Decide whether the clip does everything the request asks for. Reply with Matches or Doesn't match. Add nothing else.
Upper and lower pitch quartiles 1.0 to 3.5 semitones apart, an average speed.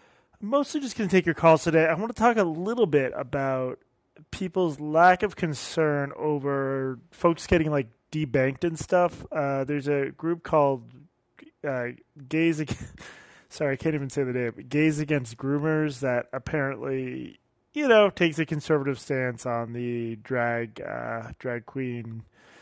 Doesn't match